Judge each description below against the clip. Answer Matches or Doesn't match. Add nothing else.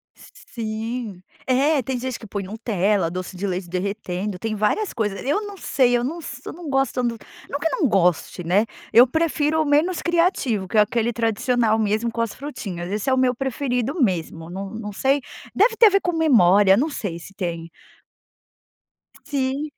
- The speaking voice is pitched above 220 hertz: Matches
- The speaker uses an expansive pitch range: Matches